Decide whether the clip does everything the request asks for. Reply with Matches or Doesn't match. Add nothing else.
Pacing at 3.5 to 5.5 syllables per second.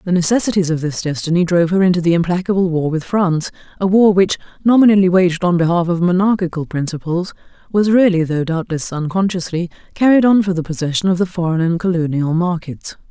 Doesn't match